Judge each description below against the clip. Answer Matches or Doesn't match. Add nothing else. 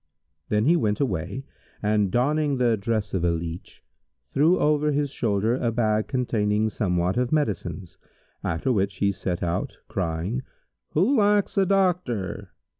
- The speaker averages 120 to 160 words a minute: Matches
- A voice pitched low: Matches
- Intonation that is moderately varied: Doesn't match